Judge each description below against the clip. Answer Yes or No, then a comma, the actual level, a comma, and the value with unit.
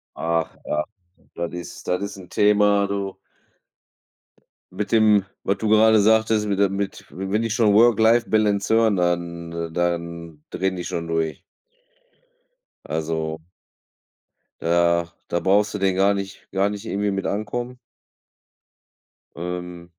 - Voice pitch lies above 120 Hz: No, very low, 95 Hz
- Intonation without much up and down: No, average, 3.4 semitones